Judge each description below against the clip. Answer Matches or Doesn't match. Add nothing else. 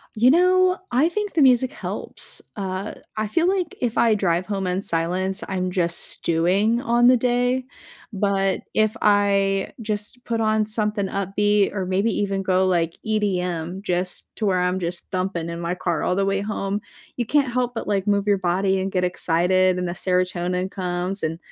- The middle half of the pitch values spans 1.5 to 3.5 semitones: Matches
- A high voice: Matches